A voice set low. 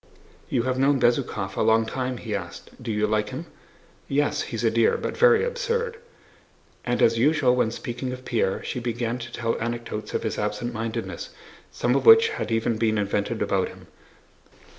Yes: low, 120 Hz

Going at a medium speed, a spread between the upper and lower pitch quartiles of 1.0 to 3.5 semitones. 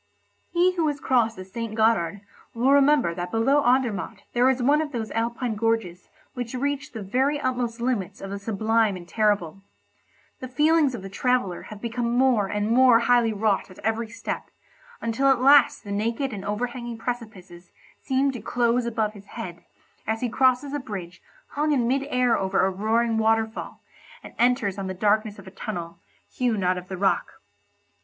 No: average, 180 wpm; average, 4.0 semitones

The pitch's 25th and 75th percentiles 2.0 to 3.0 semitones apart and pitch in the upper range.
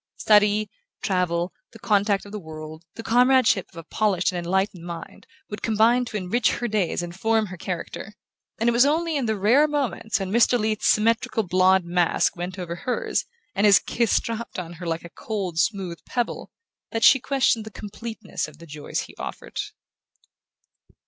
No: average, 4.3 semitones; high, 205 Hz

